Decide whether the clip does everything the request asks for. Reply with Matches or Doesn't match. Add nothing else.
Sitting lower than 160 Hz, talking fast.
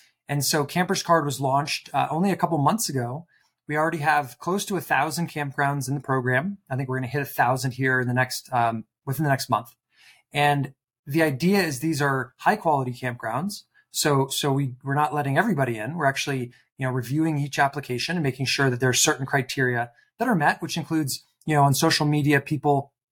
Matches